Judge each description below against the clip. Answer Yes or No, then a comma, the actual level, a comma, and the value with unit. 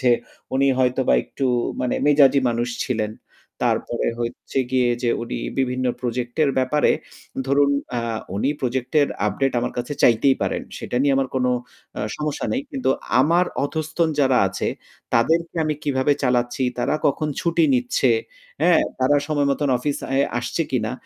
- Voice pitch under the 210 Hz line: Yes, low, 135 Hz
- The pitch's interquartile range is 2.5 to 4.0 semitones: Yes, average, 3.1 semitones